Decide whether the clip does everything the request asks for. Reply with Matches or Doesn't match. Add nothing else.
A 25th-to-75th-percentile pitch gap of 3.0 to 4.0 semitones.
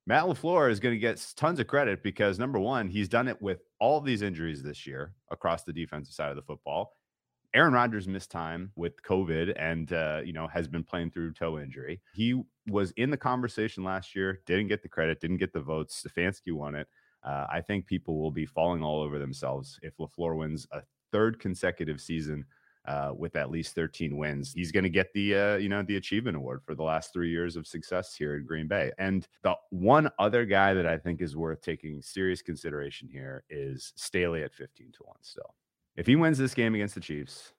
Doesn't match